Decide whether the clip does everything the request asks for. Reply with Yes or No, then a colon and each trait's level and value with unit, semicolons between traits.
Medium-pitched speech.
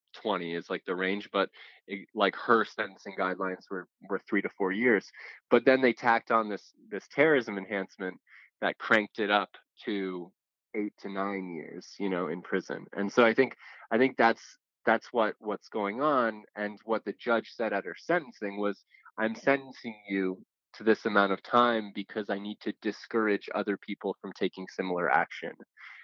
No: low, 100 Hz